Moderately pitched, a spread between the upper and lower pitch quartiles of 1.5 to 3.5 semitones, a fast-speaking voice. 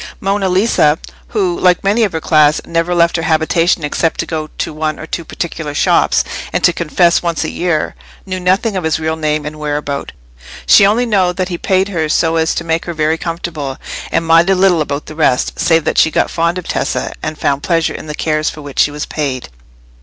Yes: medium, 165 Hz; average, 2.7 semitones; fast, 220 wpm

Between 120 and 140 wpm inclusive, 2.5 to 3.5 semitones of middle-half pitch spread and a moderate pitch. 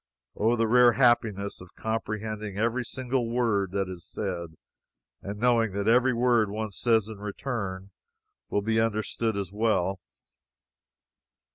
No: slow, 135 wpm; average, 2.9 semitones; low, 110 Hz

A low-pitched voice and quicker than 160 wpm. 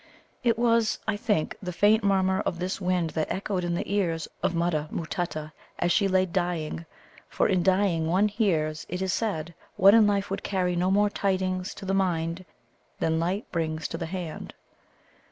No: medium, 185 Hz; average, 185 wpm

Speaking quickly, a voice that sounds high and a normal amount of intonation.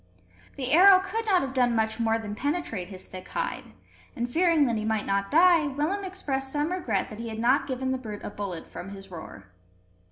No: fast, 215 wpm; very high, 255 Hz; wide, 7.1 semitones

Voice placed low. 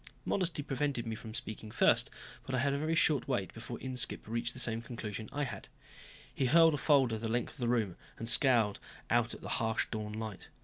Yes: low, 120 Hz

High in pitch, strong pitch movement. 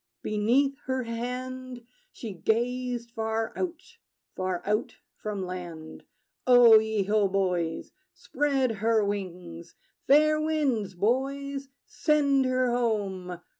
No: high, 230 Hz; average, 4.9 semitones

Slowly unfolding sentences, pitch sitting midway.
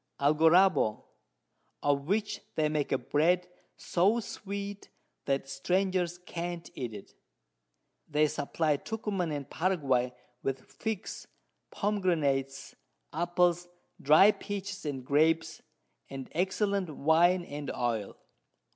Yes: slow, 100 wpm; medium, 165 Hz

